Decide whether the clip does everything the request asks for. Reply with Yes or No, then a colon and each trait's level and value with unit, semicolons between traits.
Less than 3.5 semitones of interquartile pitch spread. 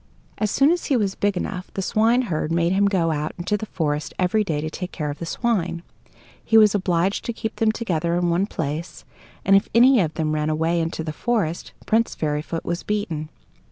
No: average, 4.8 semitones